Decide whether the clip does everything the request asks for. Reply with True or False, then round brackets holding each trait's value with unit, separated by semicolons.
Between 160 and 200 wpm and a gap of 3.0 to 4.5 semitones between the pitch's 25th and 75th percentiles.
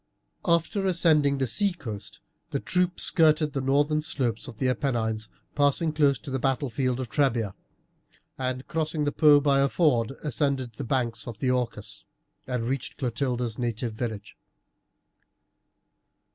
False (145 wpm; 3.9 semitones)